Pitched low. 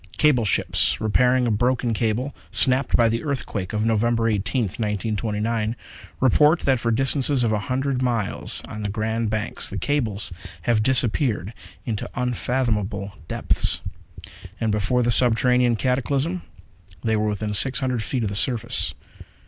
Yes: low, 115 Hz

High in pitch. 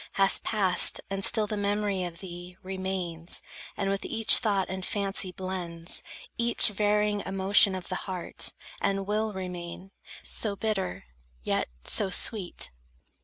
Yes: high, 195 Hz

